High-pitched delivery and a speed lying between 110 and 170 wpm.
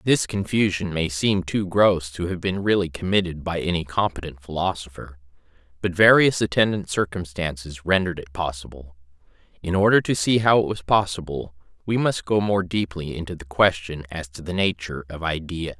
No: very low, 90 Hz; average, 165 wpm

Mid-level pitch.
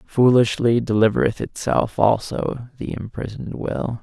No: low, 115 Hz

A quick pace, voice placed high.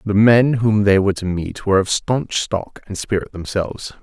No: fast, 210 wpm; low, 105 Hz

